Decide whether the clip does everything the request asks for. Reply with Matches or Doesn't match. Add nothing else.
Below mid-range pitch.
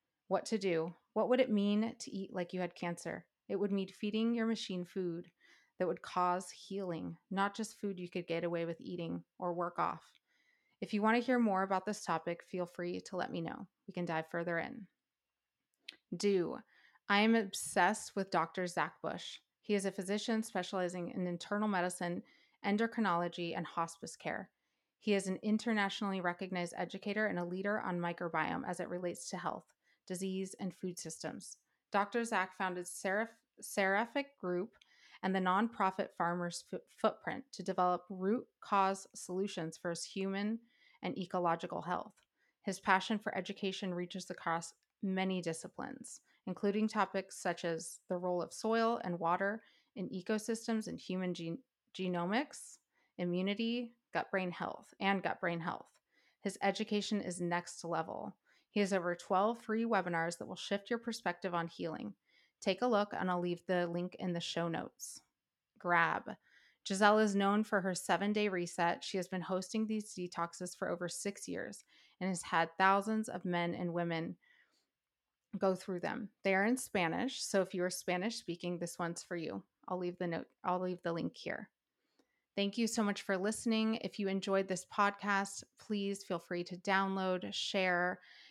Doesn't match